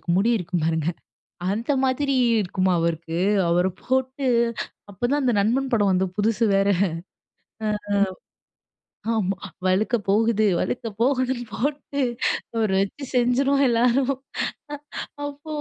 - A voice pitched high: Yes, high, 230 Hz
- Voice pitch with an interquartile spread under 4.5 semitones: No, average, 5.2 semitones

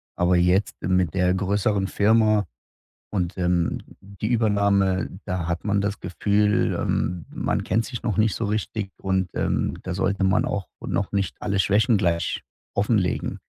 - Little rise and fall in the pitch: Yes, narrow, 2.3 semitones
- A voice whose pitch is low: Yes, low, 100 Hz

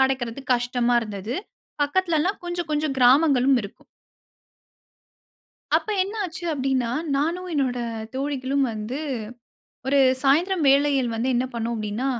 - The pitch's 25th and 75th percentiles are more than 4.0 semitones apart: No, average, 3.6 semitones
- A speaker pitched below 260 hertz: No, very high, 270 Hz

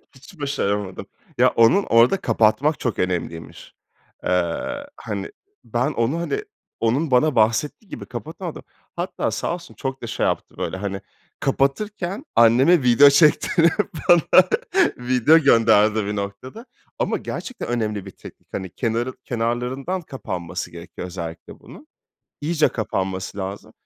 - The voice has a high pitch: No, low, 120 Hz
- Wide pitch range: Yes, wide, 6.7 semitones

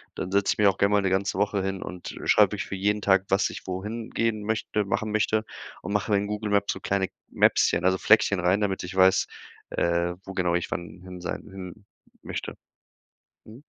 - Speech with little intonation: Yes, narrow, 2.0 semitones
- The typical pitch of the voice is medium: No, low, 100 Hz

